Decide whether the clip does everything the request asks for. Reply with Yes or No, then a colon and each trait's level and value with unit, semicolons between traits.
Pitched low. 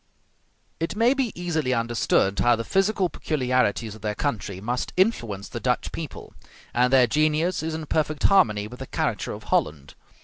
Yes: low, 130 Hz